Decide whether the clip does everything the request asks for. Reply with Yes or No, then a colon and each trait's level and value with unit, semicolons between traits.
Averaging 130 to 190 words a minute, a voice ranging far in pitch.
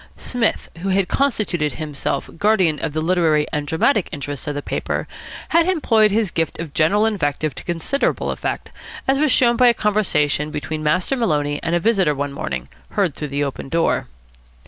Yes: average, 180 wpm; wide, 6.3 semitones